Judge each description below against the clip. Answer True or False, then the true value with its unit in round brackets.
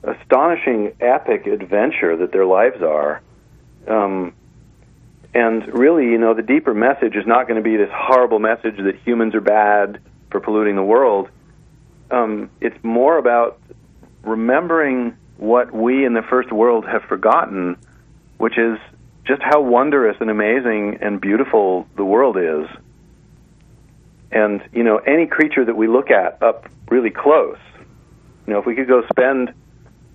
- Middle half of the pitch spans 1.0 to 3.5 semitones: True (3.1 semitones)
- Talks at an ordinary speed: True (150 wpm)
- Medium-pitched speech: False (115 Hz)